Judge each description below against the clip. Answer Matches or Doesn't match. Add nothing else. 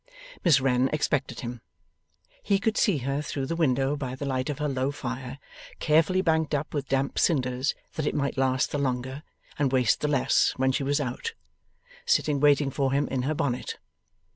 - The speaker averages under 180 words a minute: Doesn't match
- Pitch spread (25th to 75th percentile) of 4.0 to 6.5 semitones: Doesn't match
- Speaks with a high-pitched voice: Doesn't match